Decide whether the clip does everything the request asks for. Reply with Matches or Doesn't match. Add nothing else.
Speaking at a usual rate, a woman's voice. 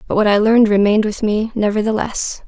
Matches